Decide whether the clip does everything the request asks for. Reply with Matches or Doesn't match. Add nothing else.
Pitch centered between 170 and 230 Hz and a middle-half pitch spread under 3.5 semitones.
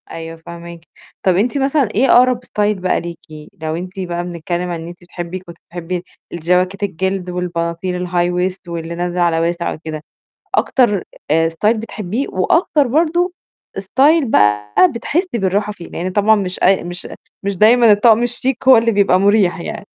Doesn't match